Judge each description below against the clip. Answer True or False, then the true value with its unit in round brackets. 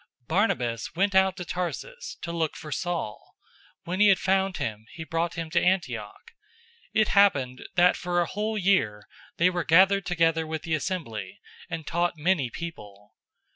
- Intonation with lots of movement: False (3.4 semitones)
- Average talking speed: True (175 wpm)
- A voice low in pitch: False (175 Hz)